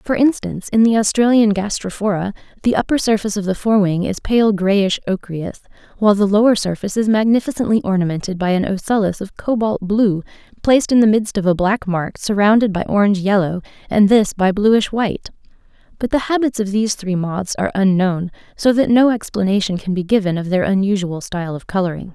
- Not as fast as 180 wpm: No, average, 185 wpm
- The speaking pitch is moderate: No, high, 205 Hz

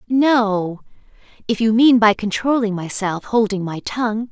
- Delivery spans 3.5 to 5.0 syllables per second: Yes, 4.3 syllables/s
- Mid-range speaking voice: No, high, 220 Hz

